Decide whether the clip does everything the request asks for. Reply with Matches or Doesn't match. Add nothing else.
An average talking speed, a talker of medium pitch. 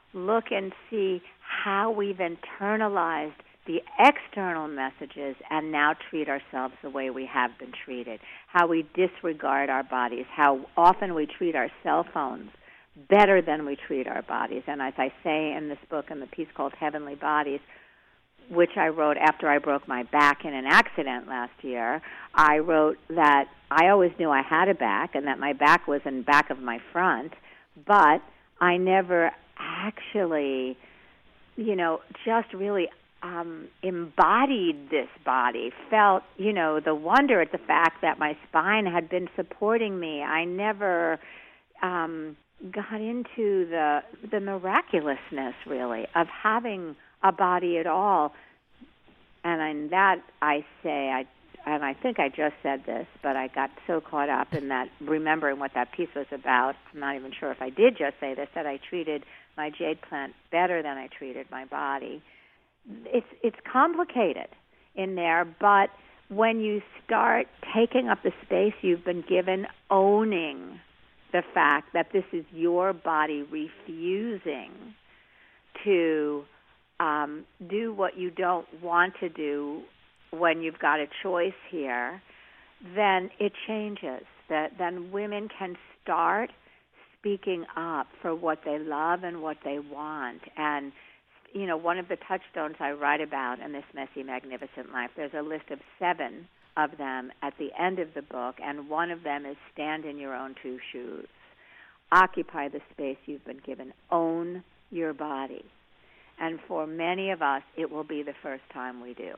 Matches